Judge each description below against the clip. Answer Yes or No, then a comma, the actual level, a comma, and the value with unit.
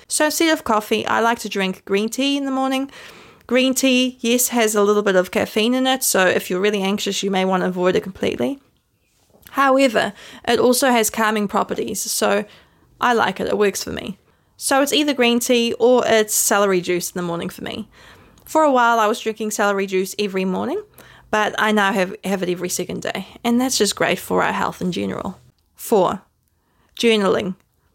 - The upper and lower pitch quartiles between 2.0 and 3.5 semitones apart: No, average, 3.9 semitones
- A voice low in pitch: No, high, 220 Hz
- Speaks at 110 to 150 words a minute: No, average, 200 wpm